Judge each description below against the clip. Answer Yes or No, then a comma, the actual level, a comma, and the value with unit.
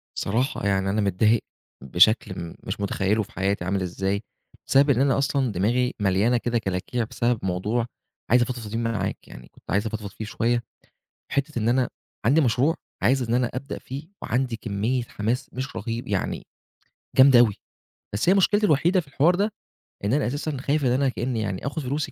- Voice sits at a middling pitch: No, low, 120 Hz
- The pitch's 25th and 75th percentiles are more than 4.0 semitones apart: Yes, average, 4.7 semitones